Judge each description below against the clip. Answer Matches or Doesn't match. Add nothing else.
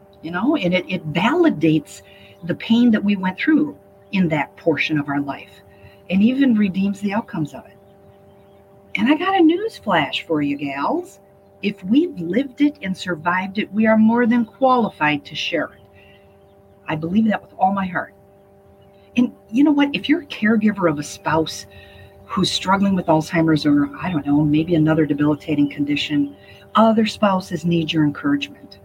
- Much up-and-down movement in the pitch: Matches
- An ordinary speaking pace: Matches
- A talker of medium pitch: Matches